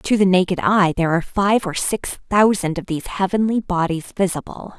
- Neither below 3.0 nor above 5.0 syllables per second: No, 5.5 syllables/s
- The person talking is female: Yes, female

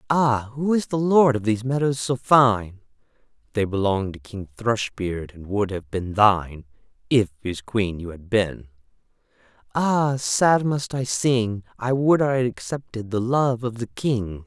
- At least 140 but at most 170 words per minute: Yes, average, 165 wpm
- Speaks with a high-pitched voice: No, low, 115 Hz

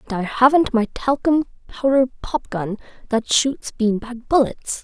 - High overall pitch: Yes, high, 245 Hz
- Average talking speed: Yes, average, 160 wpm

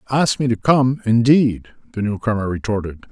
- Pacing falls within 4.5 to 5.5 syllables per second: No, 5.7 syllables/s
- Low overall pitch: Yes, low, 115 Hz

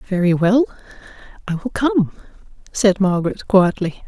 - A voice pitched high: Yes, high, 200 Hz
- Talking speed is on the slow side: Yes, slow, 120 wpm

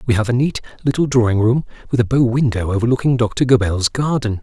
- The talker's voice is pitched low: Yes, low, 120 Hz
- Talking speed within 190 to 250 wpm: Yes, fast, 205 wpm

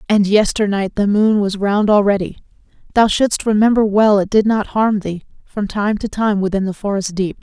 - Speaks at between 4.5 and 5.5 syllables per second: Yes, 5.0 syllables/s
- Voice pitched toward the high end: Yes, high, 205 Hz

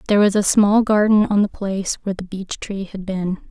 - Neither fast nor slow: No, fast, 240 wpm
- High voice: Yes, high, 200 Hz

